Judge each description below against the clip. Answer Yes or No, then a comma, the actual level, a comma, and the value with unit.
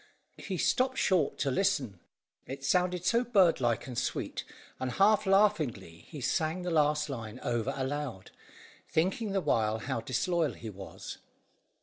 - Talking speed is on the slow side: No, average, 145 wpm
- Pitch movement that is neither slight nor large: No, wide, 7.6 semitones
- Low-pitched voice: No, medium, 150 Hz